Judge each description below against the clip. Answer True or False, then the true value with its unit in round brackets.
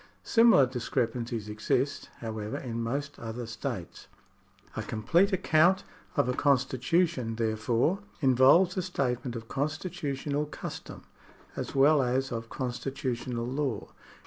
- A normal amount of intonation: True (4.0 semitones)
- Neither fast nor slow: False (115 wpm)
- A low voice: True (130 Hz)